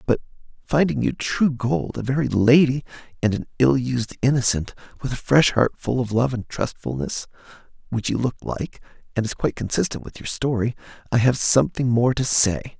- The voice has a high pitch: No, low, 120 Hz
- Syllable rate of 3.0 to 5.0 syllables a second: No, 5.2 syllables/s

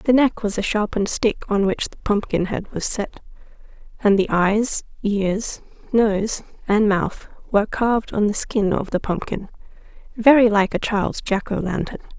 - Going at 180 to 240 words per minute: No, average, 165 wpm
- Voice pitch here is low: No, high, 210 Hz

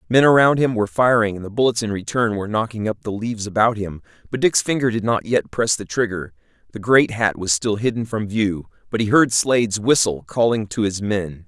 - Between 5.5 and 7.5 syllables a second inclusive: Yes, 5.6 syllables/s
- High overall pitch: No, low, 110 Hz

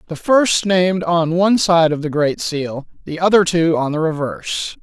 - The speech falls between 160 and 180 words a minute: No, average, 200 wpm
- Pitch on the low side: No, medium, 170 Hz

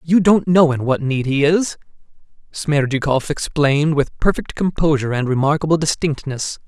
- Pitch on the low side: No, medium, 150 Hz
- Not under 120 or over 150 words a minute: Yes, average, 145 wpm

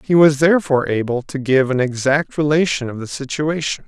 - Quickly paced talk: No, average, 185 wpm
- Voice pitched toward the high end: No, medium, 140 Hz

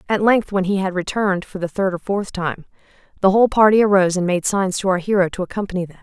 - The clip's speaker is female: Yes, female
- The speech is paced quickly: Yes, fast, 250 wpm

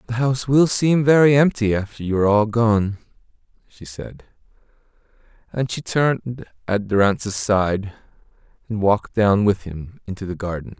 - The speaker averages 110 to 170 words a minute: Yes, average, 150 wpm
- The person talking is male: Yes, male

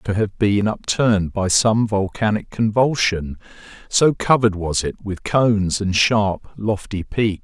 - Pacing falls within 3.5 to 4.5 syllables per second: Yes, 4.1 syllables/s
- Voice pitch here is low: Yes, low, 105 Hz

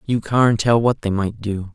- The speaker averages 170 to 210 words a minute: No, fast, 240 wpm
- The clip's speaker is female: No, male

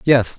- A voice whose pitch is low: Yes, low, 130 Hz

